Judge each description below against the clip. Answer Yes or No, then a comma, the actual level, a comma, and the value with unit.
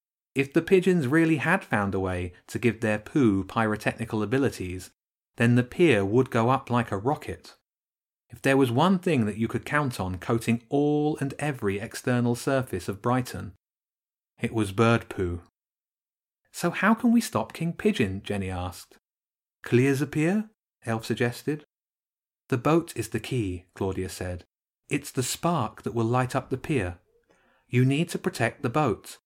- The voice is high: No, low, 120 Hz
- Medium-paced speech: Yes, average, 165 wpm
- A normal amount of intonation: No, wide, 5.7 semitones